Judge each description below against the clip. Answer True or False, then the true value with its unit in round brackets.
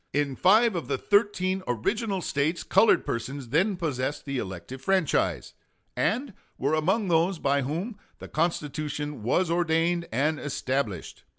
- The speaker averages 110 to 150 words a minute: True (135 wpm)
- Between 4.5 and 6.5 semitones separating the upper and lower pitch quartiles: True (5.2 semitones)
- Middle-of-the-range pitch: True (155 Hz)